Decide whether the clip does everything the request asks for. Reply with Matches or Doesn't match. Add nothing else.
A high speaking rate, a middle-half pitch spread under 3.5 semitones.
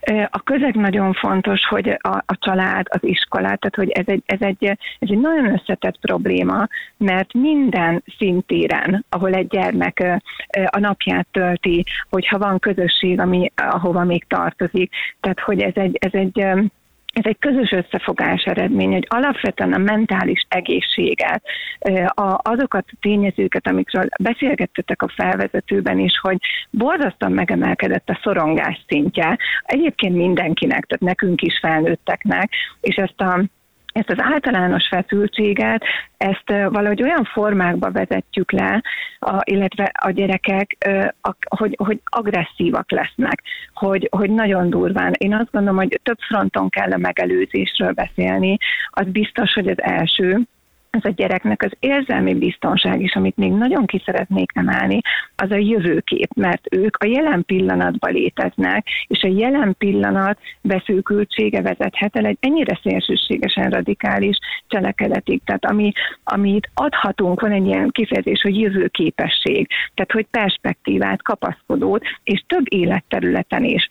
Doesn't match